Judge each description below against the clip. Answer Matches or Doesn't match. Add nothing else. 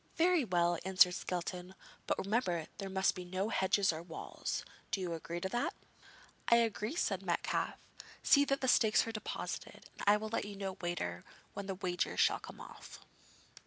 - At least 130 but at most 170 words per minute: Doesn't match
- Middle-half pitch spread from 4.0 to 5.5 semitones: Doesn't match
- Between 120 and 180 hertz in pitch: Doesn't match